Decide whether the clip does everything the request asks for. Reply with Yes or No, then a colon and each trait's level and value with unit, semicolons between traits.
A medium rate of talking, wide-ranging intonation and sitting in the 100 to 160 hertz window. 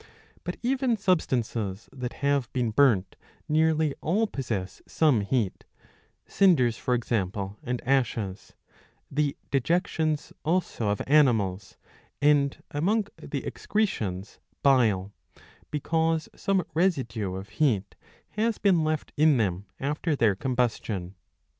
No: slow, 110 wpm; wide, 6.9 semitones; low, 135 Hz